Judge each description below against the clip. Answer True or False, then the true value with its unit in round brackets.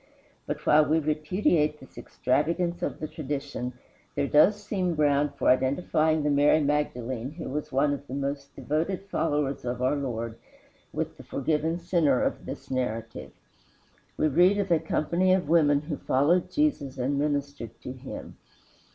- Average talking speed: True (160 wpm)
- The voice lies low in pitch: False (150 Hz)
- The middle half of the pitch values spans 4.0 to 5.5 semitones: False (2.9 semitones)